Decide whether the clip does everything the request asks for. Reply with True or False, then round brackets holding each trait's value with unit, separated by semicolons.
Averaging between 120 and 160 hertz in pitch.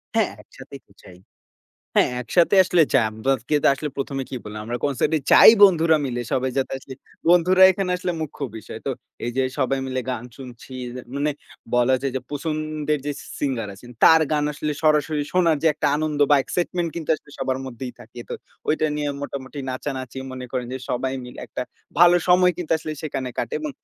True (140 Hz)